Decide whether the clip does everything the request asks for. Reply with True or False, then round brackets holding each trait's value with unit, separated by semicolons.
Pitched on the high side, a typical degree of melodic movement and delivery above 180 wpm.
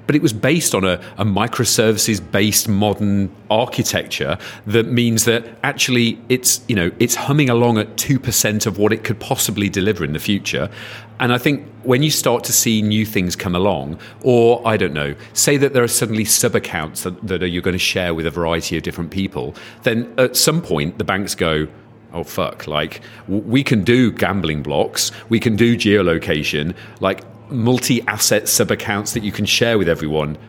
False (110 Hz; 3.6 semitones; 195 wpm)